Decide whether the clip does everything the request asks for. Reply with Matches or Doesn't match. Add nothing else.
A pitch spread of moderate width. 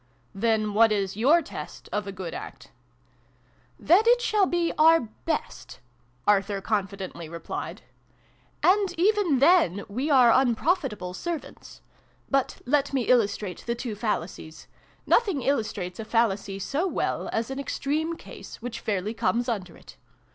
Doesn't match